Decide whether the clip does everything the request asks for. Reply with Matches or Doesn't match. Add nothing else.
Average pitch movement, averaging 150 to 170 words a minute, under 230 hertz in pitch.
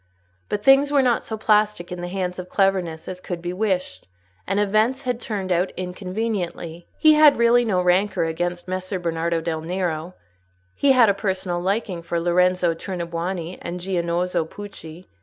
Matches